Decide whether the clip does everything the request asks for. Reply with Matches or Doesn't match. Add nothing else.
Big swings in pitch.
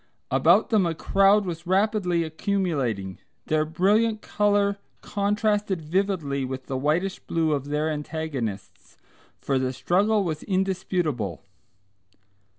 Matches